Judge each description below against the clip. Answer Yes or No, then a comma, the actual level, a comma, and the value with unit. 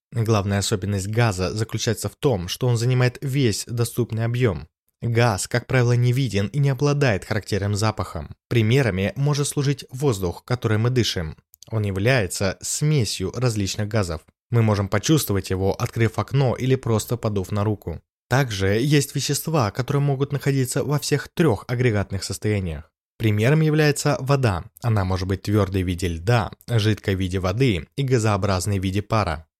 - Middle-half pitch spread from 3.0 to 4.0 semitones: No, average, 4.5 semitones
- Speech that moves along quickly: No, average, 150 wpm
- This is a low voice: Yes, low, 110 Hz